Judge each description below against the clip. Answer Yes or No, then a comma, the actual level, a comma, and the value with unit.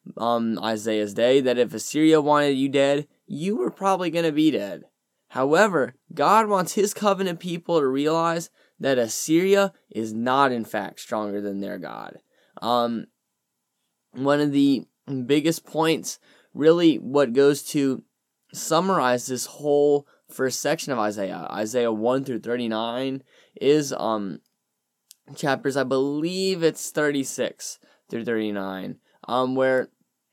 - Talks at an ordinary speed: No, slow, 130 wpm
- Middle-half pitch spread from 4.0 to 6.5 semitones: Yes, average, 5.3 semitones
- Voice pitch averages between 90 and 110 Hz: No, medium, 140 Hz